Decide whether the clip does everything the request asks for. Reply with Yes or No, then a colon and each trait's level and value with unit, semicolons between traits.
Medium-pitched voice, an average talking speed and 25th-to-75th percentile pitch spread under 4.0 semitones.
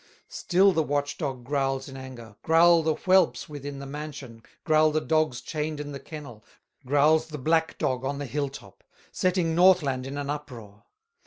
Yes: medium, 145 Hz; average, 175 wpm; average, 2.9 semitones